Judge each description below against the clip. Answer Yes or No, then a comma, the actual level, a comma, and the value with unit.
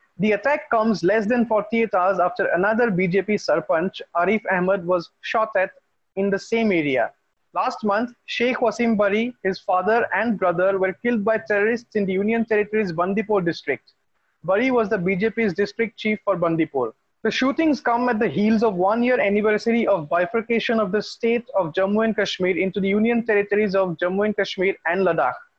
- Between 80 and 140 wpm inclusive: No, average, 180 wpm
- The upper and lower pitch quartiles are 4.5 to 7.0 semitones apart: No, average, 3.2 semitones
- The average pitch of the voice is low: No, high, 210 Hz